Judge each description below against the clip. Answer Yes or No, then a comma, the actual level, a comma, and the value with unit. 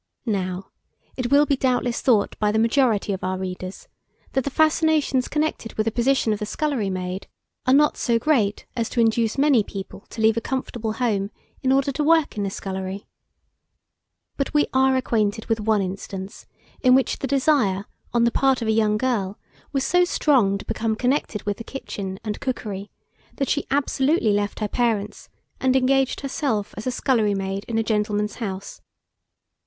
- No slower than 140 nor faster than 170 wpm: No, average, 180 wpm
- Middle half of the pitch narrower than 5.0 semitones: Yes, average, 4.6 semitones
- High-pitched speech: Yes, high, 225 Hz